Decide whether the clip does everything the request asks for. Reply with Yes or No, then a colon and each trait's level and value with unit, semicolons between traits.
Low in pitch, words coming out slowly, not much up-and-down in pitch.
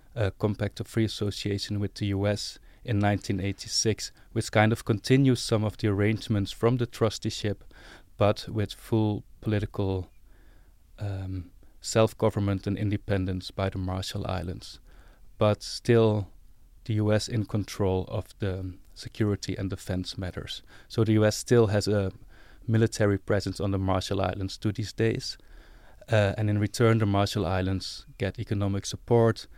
Yes: low, 105 Hz; slow, 140 wpm; narrow, 2.3 semitones